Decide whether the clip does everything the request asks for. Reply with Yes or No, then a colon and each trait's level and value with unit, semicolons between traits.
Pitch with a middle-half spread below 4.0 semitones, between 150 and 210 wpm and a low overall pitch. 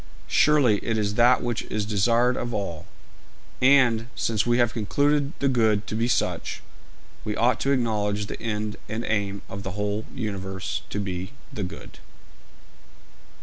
Yes: average, 2.9 semitones; average, 155 wpm; low, 110 Hz